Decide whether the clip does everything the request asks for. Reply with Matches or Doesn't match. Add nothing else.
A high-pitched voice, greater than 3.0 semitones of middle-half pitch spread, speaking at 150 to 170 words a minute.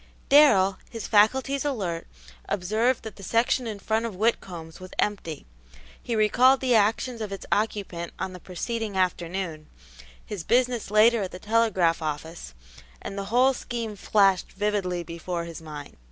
Matches